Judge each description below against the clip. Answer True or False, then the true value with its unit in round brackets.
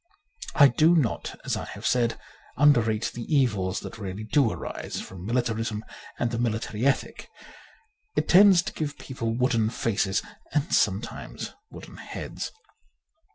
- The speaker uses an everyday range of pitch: True (4.1 semitones)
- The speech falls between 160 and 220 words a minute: False (145 wpm)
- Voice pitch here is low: True (115 Hz)